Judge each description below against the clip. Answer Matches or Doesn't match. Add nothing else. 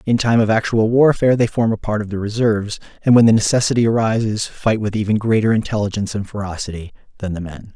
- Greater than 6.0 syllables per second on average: Matches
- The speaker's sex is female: Doesn't match